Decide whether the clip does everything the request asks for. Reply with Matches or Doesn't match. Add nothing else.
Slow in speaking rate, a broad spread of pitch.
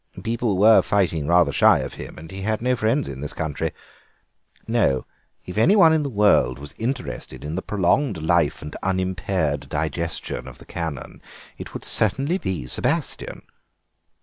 Doesn't match